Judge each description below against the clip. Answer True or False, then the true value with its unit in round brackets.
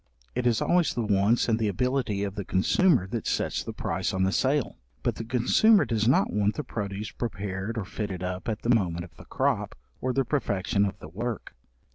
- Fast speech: True (210 wpm)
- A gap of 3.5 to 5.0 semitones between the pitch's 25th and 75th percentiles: True (3.8 semitones)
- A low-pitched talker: True (110 Hz)